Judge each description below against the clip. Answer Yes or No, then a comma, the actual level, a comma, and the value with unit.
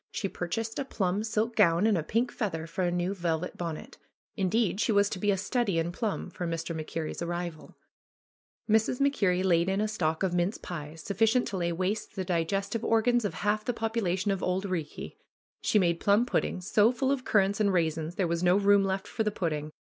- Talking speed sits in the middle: No, fast, 215 wpm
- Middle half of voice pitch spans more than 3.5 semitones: Yes, average, 3.9 semitones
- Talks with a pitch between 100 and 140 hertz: No, high, 190 Hz